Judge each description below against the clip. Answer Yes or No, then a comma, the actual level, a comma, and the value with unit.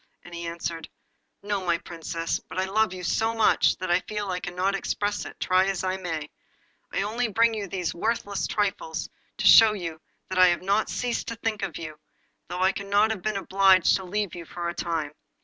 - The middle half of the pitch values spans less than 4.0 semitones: Yes, average, 3.1 semitones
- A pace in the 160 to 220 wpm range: Yes, average, 200 wpm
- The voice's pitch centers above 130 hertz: Yes, high, 190 Hz